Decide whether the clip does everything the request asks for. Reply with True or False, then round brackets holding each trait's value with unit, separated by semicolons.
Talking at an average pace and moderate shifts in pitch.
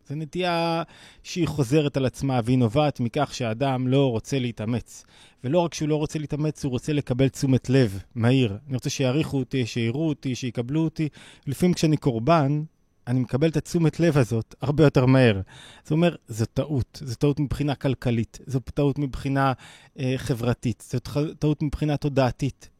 False (165 wpm; 3.4 semitones)